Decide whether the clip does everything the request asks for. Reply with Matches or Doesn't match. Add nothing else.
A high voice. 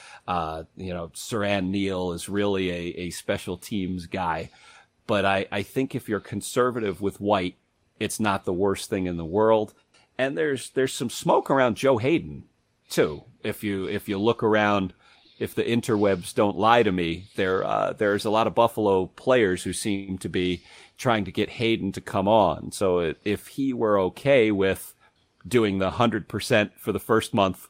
Doesn't match